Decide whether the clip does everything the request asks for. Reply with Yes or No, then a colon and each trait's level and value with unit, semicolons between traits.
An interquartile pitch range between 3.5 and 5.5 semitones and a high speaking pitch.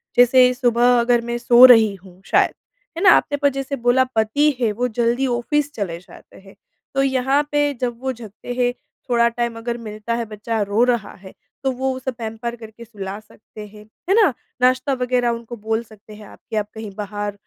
No: average, 2.7 semitones; high, 235 Hz